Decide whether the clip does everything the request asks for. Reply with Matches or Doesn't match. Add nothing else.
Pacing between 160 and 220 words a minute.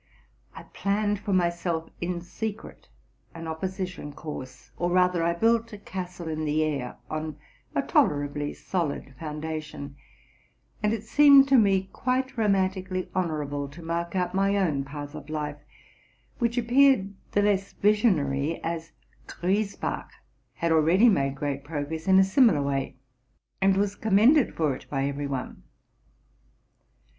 Doesn't match